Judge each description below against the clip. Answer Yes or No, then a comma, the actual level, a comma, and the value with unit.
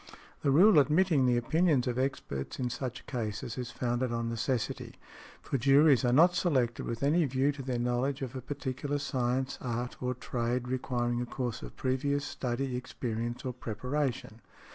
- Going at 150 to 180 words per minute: Yes, average, 165 wpm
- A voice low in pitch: Yes, low, 130 Hz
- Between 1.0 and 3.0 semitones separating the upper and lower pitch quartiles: Yes, narrow, 2.5 semitones